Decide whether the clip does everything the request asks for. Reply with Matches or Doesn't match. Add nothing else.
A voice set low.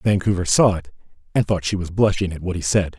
Matches